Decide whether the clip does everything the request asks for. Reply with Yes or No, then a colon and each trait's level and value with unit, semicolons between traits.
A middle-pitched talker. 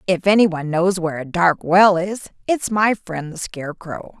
Yes: medium, 180 Hz